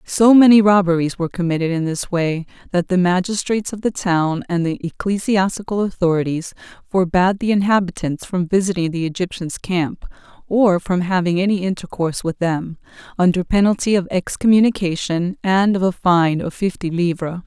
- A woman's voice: Yes, female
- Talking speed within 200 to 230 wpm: No, average, 150 wpm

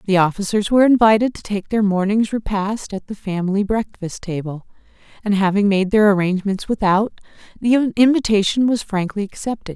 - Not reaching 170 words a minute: Yes, average, 155 wpm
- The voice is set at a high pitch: Yes, high, 205 Hz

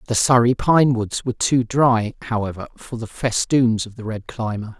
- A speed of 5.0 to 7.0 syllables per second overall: No, 4.8 syllables/s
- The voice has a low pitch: Yes, low, 115 Hz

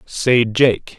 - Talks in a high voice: No, low, 120 Hz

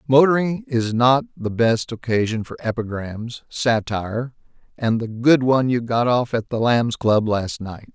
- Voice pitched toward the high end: No, low, 120 Hz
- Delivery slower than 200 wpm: Yes, average, 165 wpm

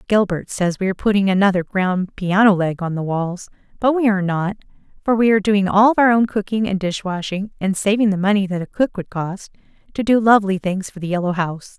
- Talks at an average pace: No, fast, 220 wpm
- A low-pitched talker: No, high, 195 Hz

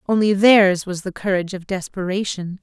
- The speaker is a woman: Yes, female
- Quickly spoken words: No, average, 160 wpm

